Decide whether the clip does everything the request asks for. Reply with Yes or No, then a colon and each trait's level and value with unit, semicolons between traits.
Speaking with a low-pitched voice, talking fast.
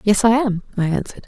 No: high, 210 Hz; fast, 235 wpm